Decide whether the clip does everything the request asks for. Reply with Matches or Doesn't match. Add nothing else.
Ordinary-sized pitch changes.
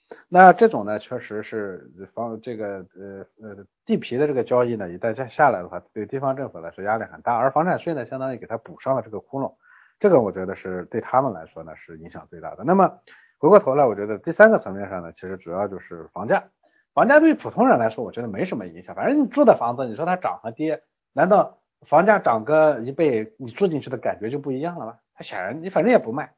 Doesn't match